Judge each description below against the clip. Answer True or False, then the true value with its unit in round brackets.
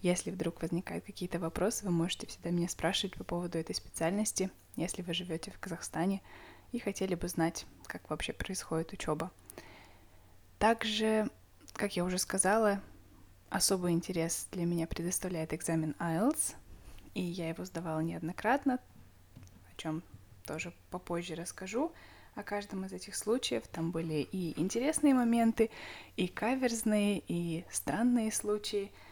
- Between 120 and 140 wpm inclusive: True (130 wpm)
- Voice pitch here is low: False (175 Hz)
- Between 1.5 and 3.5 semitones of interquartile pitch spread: False (4.0 semitones)